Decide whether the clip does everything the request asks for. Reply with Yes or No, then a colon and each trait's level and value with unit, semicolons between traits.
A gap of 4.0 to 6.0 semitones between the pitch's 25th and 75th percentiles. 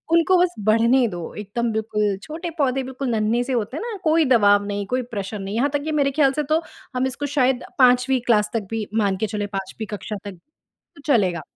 Yes: average, 4.5 semitones